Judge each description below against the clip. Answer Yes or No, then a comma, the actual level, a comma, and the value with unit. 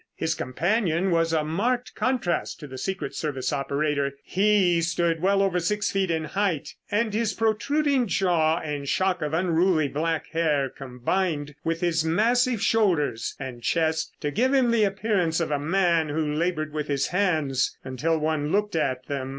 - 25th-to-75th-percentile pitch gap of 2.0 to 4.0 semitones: No, average, 4.7 semitones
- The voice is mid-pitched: Yes, medium, 165 Hz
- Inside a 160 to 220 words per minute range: Yes, average, 165 wpm